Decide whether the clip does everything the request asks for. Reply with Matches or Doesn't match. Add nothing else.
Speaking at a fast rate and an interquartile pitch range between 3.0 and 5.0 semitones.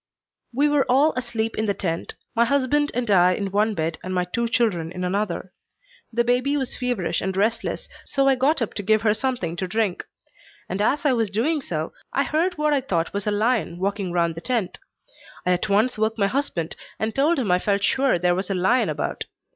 Doesn't match